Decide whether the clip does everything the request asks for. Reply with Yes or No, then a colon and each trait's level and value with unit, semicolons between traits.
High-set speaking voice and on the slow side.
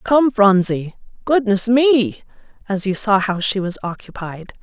Yes: high, 210 Hz; slow, 130 wpm